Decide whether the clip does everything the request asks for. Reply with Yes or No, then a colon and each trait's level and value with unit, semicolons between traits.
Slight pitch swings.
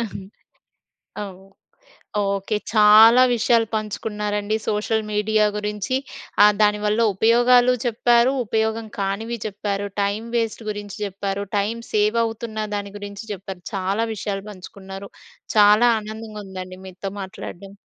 Yes: narrow, 1.9 semitones